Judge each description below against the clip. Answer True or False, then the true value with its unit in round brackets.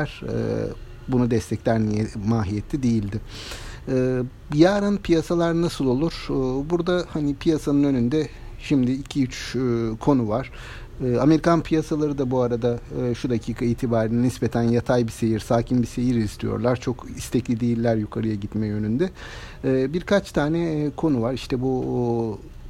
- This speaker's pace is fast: False (120 wpm)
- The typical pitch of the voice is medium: False (125 Hz)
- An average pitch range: True (3.8 semitones)